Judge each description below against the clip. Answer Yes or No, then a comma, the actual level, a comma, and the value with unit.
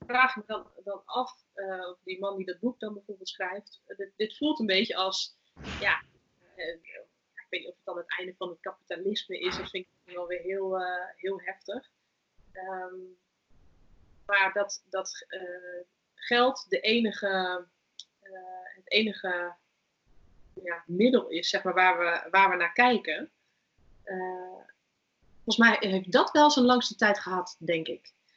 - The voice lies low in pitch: No, high, 190 Hz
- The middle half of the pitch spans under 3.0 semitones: Yes, narrow, 2.6 semitones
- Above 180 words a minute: No, average, 165 wpm